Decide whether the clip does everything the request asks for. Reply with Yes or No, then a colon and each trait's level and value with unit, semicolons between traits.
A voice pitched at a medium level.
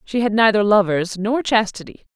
No: high, 210 Hz